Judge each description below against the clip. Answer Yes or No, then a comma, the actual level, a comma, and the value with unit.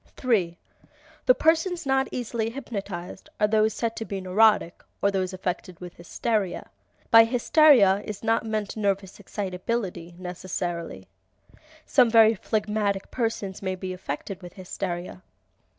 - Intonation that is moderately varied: Yes, average, 3.6 semitones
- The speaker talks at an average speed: No, slow, 130 wpm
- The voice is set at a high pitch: Yes, high, 200 Hz